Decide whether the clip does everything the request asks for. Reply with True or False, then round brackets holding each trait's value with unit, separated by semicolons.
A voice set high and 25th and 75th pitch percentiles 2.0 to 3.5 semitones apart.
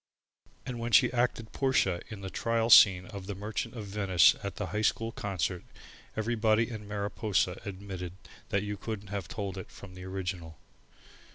False (100 Hz; 3.0 semitones)